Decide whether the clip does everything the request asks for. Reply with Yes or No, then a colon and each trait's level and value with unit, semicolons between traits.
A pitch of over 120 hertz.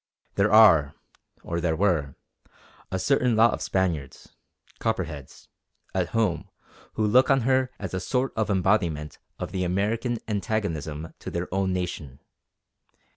No: very low, 95 Hz